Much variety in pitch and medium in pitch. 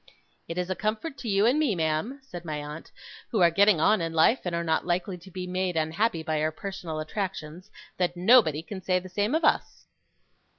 No: average, 4.2 semitones; medium, 180 Hz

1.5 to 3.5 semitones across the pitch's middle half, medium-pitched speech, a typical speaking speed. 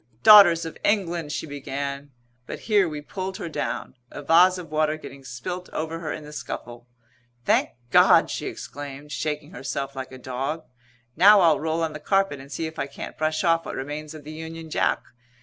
Yes: average, 2.9 semitones; medium, 155 Hz; average, 195 wpm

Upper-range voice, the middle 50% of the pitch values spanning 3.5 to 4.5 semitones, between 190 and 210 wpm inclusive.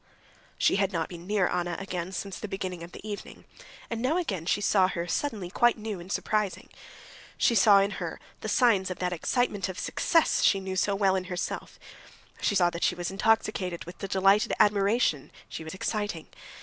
No: high, 195 Hz; average, 2.7 semitones; average, 195 wpm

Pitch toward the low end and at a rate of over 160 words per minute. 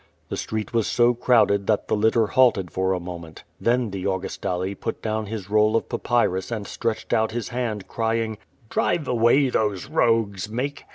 Yes: low, 110 Hz; average, 175 wpm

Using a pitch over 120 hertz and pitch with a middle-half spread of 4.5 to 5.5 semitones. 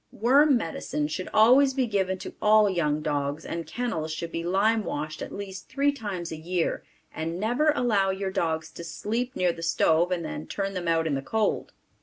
Yes: medium, 185 Hz; average, 5.2 semitones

